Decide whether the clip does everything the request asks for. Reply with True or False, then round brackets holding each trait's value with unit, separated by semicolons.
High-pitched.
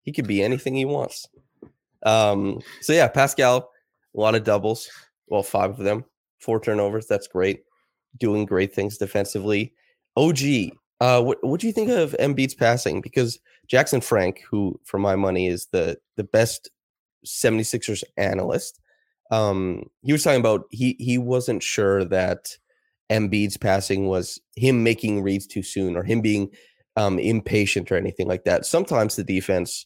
False (110 Hz)